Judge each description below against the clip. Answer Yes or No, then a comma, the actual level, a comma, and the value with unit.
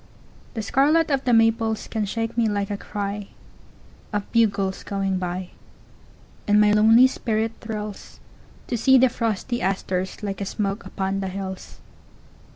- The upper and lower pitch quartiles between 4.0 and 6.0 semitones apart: No, narrow, 2.6 semitones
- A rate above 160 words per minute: No, slow, 135 wpm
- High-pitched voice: Yes, high, 210 Hz